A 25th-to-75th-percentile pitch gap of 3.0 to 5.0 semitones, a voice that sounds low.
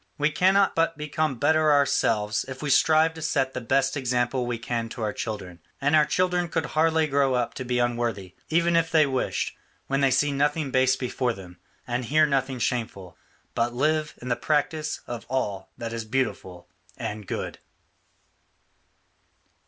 Yes: average, 4.5 semitones; low, 130 Hz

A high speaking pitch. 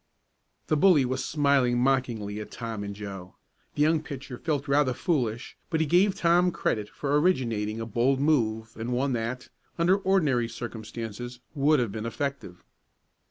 No: low, 125 Hz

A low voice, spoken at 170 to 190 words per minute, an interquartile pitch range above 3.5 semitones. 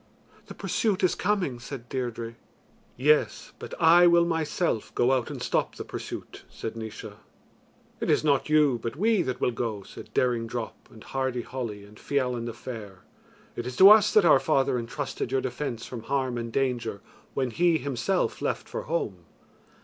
Yes: low, 130 Hz; average, 175 wpm; average, 4.4 semitones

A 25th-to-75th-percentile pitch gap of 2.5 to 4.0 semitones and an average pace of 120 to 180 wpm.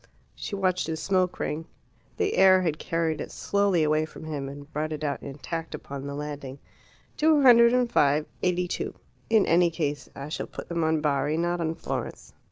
No: average, 3.6 semitones; average, 190 wpm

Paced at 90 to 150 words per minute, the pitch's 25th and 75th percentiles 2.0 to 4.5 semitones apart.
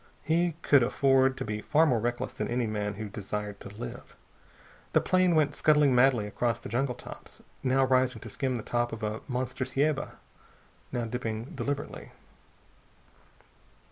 No: average, 160 wpm; average, 3.6 semitones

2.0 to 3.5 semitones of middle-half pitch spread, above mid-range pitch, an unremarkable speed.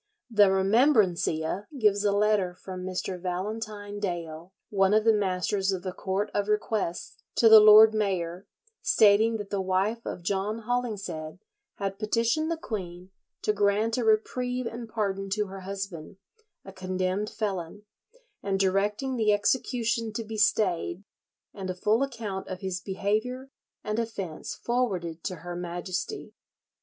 Yes: average, 2.8 semitones; high, 205 Hz; average, 150 wpm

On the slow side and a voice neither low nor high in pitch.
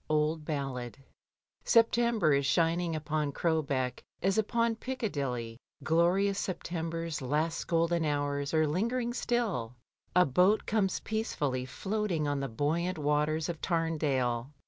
Yes: slow, 120 wpm; medium, 160 Hz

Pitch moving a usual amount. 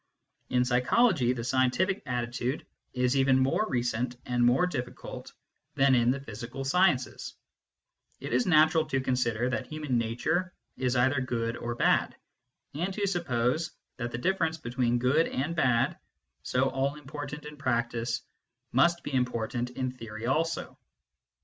Yes: average, 3.6 semitones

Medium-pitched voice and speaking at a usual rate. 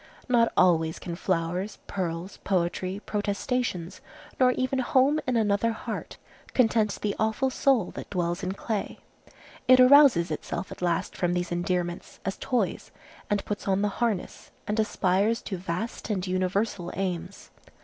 No: high, 195 Hz; average, 145 wpm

